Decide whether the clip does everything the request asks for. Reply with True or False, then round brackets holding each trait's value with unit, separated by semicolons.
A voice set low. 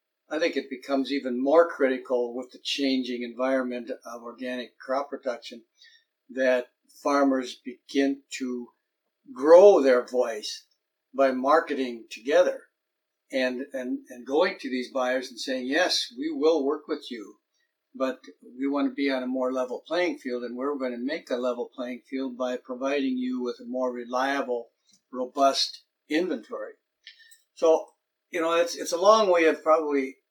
True (130 Hz)